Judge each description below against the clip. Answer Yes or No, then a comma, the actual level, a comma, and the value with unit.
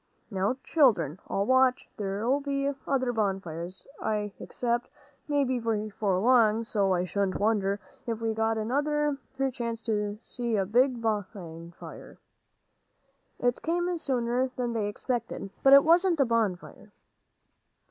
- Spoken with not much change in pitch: No, average, 4.2 semitones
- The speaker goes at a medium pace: No, slow, 125 wpm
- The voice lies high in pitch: Yes, high, 225 Hz